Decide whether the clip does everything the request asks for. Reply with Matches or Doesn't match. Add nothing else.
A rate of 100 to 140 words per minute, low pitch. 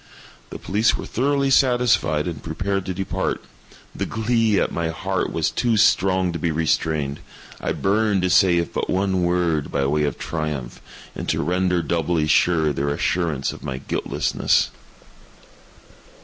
Doesn't match